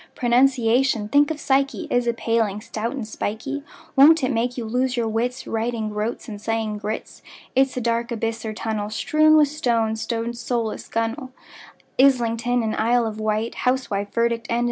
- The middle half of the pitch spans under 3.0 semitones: Yes, narrow, 2.5 semitones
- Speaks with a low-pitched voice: No, high, 235 Hz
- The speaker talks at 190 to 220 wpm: No, average, 170 wpm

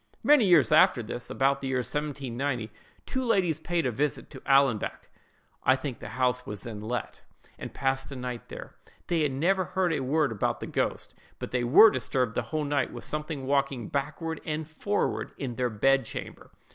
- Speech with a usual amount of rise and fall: Yes, average, 3.8 semitones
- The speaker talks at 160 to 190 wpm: Yes, average, 185 wpm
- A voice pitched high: No, low, 135 Hz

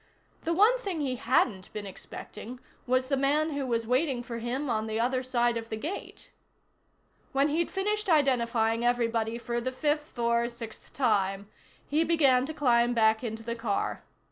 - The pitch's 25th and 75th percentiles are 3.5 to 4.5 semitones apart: Yes, average, 3.9 semitones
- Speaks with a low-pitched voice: No, high, 245 Hz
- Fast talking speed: No, average, 170 wpm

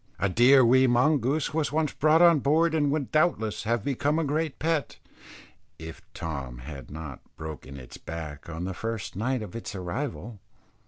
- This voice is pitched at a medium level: No, low, 120 Hz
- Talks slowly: No, average, 170 wpm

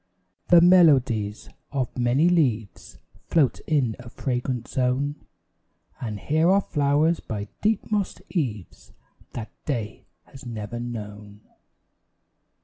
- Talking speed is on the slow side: Yes, slow, 110 wpm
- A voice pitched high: No, low, 125 Hz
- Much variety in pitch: Yes, wide, 5.8 semitones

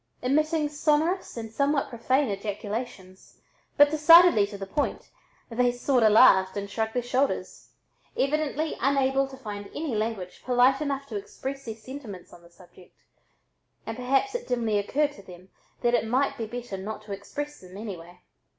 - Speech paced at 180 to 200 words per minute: No, average, 160 wpm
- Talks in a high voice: Yes, high, 245 Hz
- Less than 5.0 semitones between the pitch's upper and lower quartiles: No, wide, 5.4 semitones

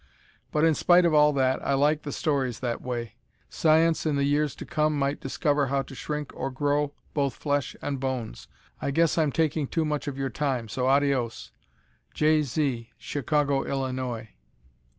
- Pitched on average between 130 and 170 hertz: Yes, medium, 140 Hz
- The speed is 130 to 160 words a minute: No, average, 175 wpm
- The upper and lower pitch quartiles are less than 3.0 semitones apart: Yes, narrow, 2.4 semitones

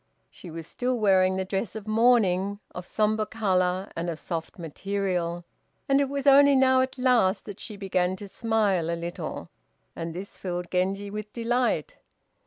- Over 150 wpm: Yes, average, 170 wpm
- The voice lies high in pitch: Yes, high, 200 Hz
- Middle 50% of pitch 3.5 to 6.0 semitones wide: Yes, average, 4.1 semitones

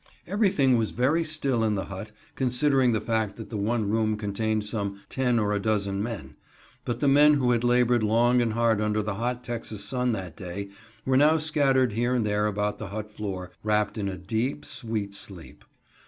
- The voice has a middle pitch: No, low, 110 Hz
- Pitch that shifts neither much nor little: Yes, average, 3.1 semitones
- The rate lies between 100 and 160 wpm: No, average, 200 wpm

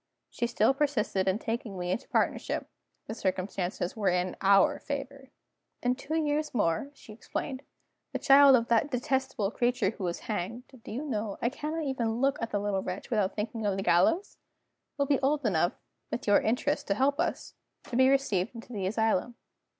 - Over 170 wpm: Yes, average, 185 wpm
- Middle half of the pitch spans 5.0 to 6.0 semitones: Yes, wide, 5.5 semitones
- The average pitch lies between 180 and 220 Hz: No, high, 230 Hz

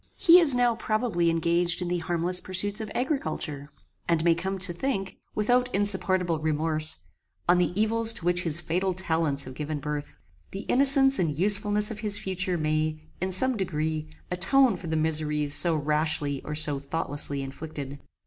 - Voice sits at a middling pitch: Yes, medium, 175 Hz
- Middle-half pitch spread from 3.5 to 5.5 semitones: Yes, average, 4.8 semitones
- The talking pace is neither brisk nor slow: Yes, average, 170 wpm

